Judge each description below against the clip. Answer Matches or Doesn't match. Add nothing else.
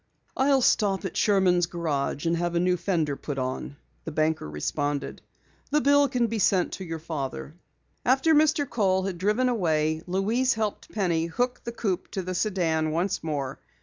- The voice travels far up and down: Matches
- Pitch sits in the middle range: Matches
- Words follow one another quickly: Doesn't match